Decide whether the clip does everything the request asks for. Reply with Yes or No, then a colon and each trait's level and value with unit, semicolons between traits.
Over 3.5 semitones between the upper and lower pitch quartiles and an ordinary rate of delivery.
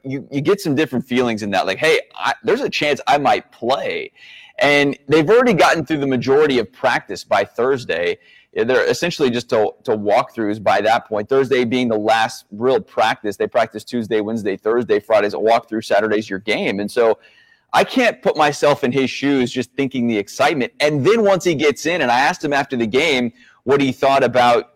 No: average, 5.0 semitones; fast, 210 wpm